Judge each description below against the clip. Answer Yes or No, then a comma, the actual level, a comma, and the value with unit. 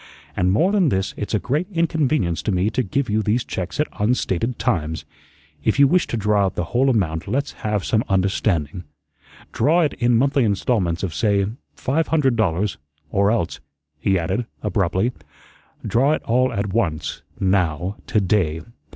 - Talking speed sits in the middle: Yes, average, 170 wpm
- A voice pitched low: Yes, low, 105 Hz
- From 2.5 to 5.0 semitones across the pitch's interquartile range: No, wide, 5.4 semitones